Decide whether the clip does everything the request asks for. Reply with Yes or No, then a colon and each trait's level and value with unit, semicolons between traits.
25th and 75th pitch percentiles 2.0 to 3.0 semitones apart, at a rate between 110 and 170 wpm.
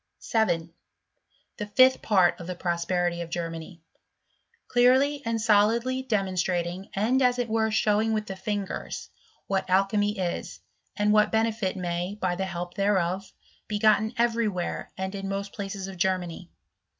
No: average, 3.5 semitones; average, 150 wpm